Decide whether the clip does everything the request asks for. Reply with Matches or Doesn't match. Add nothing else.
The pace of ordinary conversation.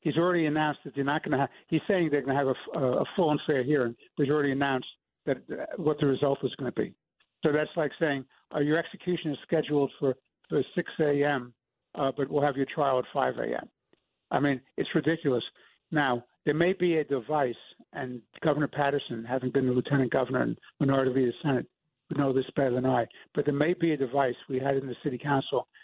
Doesn't match